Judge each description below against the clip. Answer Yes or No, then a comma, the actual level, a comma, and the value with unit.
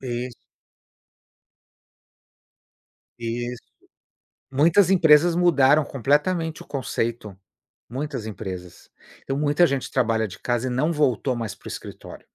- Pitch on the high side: No, low, 130 Hz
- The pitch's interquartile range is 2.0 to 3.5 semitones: No, average, 4.3 semitones